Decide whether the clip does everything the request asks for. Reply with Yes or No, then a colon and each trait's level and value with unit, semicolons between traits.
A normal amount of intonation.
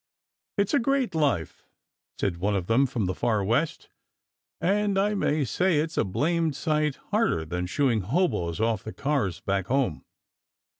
No: wide, 9.0 semitones